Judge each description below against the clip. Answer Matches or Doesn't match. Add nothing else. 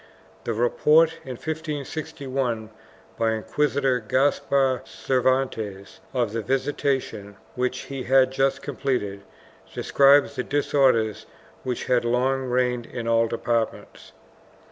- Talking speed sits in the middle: Doesn't match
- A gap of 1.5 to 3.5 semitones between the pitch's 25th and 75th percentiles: Matches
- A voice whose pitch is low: Matches